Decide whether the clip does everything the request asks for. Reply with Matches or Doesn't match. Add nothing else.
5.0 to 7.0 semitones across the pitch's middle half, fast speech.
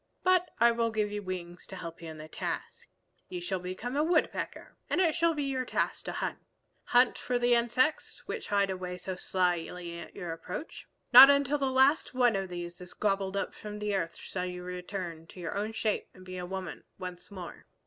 Matches